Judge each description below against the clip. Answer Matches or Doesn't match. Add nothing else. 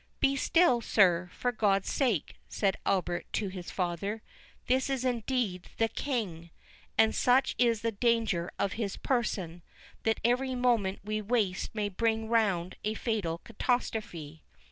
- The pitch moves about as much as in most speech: Matches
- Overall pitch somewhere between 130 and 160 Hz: Doesn't match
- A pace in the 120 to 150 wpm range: Matches